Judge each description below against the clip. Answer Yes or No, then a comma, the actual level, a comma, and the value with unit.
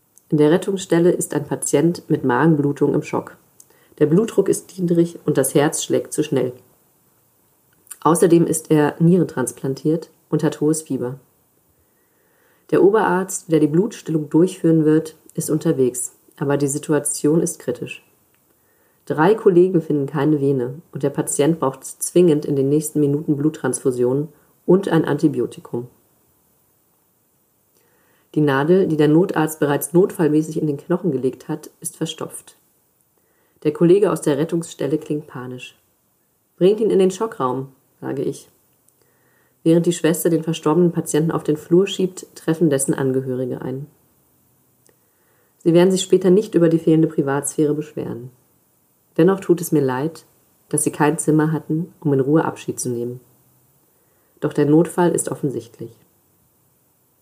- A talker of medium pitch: Yes, medium, 155 Hz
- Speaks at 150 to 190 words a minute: No, average, 140 wpm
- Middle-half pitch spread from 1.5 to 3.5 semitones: Yes, average, 2.8 semitones